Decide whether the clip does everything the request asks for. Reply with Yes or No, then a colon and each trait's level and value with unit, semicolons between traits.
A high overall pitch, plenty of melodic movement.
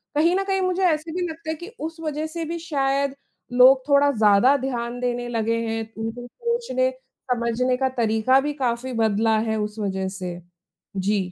Yes: very high, 255 Hz; wide, 5.7 semitones